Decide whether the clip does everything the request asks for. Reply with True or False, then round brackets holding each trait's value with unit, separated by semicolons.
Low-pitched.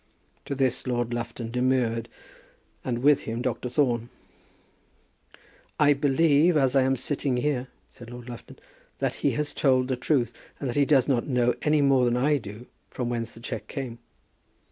True (125 Hz)